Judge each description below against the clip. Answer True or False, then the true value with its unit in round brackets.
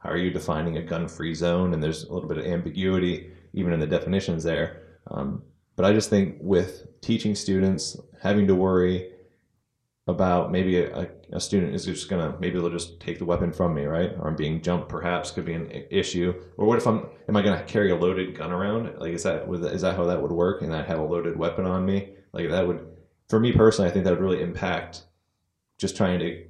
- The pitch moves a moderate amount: False (1.9 semitones)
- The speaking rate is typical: False (225 wpm)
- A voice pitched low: True (90 Hz)